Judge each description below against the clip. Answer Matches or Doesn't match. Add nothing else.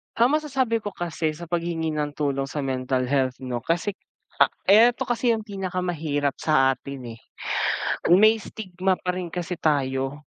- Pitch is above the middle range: Doesn't match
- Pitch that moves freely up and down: Matches